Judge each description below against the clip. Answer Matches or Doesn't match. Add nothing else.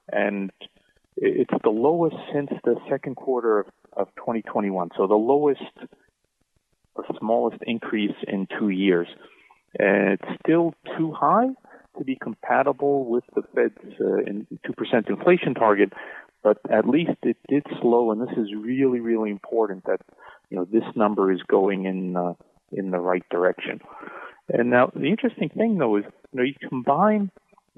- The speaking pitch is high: Doesn't match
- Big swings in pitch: Matches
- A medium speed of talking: Matches